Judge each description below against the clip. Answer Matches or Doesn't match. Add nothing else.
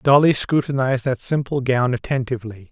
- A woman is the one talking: Doesn't match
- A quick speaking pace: Doesn't match